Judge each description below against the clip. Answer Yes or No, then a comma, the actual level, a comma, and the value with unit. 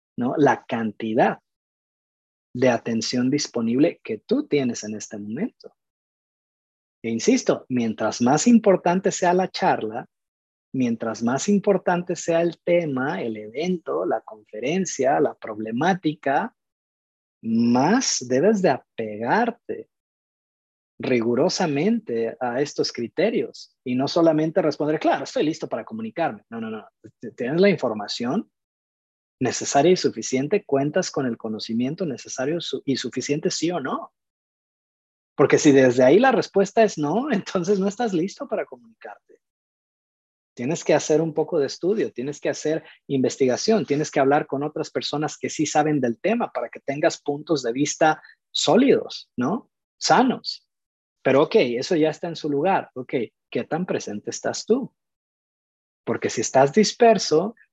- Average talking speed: Yes, average, 135 wpm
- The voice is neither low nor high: Yes, medium, 145 Hz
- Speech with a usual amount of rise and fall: No, wide, 7.7 semitones